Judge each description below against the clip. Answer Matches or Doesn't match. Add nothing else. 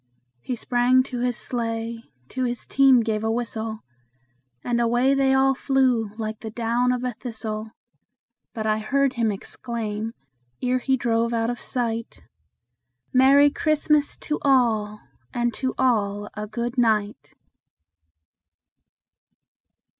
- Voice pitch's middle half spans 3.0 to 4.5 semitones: Doesn't match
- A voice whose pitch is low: Doesn't match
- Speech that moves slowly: Matches